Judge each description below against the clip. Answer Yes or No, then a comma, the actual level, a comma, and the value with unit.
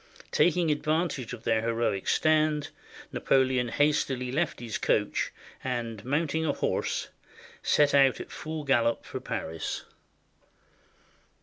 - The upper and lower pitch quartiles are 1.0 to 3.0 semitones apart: No, average, 4.5 semitones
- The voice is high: No, low, 135 Hz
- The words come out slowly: Yes, slow, 120 wpm